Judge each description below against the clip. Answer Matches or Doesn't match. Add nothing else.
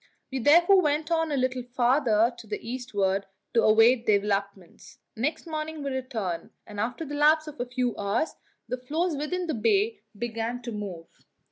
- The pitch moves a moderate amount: Doesn't match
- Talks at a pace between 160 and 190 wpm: Matches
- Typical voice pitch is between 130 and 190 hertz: Doesn't match